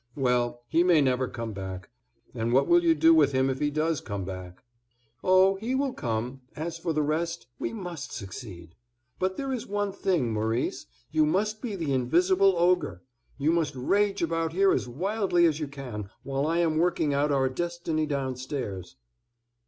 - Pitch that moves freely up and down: Yes, wide, 6.3 semitones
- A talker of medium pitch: Yes, medium, 155 Hz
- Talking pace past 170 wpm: Yes, average, 180 wpm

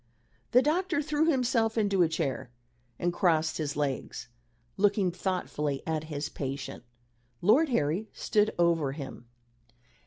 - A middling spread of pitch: No, wide, 6.9 semitones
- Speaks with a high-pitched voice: No, medium, 175 Hz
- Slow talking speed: Yes, slow, 125 wpm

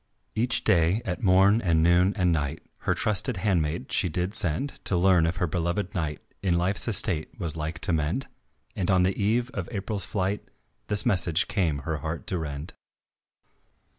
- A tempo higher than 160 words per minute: Yes, average, 175 wpm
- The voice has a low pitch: Yes, very low, 90 Hz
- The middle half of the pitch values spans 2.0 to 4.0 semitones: Yes, average, 3.6 semitones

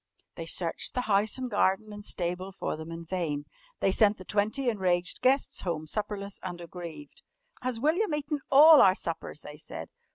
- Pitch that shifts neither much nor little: No, wide, 6.2 semitones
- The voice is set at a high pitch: Yes, high, 195 Hz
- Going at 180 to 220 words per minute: Yes, average, 185 wpm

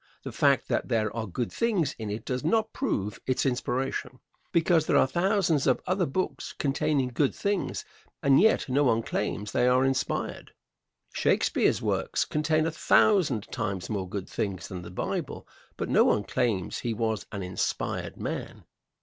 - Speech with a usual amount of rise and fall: No, wide, 6.6 semitones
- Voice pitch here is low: Yes, low, 130 Hz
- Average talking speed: Yes, average, 165 wpm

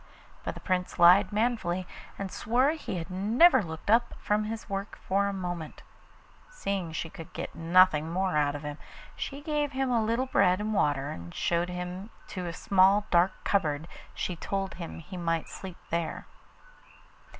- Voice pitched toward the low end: No, medium, 185 Hz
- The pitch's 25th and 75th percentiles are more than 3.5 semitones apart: Yes, average, 4.0 semitones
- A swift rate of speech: No, average, 175 wpm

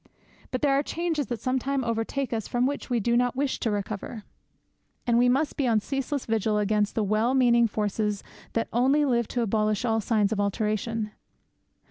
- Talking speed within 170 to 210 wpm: Yes, average, 185 wpm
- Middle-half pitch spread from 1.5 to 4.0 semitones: Yes, average, 3.3 semitones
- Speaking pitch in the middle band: No, high, 235 Hz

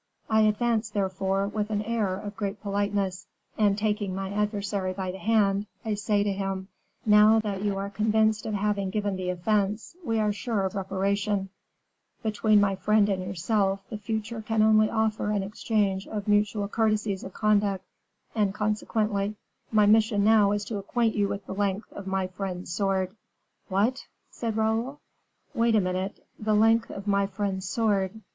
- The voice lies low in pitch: No, high, 205 Hz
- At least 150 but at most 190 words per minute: Yes, average, 170 wpm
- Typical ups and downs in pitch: No, narrow, 1.8 semitones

